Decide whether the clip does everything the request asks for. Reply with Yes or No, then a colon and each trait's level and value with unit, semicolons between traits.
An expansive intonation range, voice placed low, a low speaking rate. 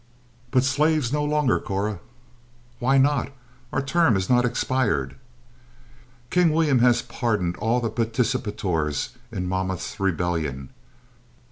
Yes: wide, 6.3 semitones; low, 115 Hz; slow, 115 wpm